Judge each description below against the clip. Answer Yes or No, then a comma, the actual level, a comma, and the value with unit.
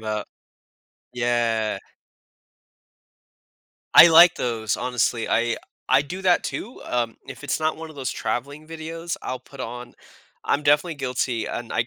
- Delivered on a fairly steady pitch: No, average, 5.0 semitones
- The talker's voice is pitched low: Yes, low, 130 Hz